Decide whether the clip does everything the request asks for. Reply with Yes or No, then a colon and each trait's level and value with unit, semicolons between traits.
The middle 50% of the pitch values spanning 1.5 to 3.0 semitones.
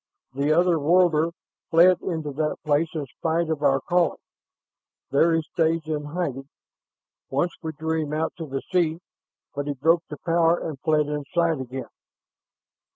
Yes: narrow, 2.4 semitones